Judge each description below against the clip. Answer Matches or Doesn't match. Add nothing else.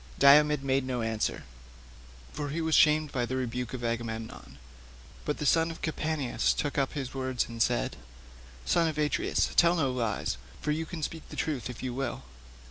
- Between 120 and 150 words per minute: Doesn't match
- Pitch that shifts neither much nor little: Matches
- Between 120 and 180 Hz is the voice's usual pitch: Matches